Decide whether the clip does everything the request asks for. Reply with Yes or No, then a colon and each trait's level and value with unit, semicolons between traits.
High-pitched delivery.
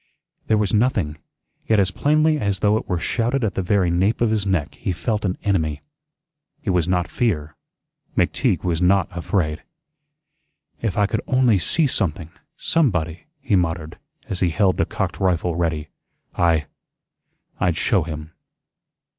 No: very low, 95 Hz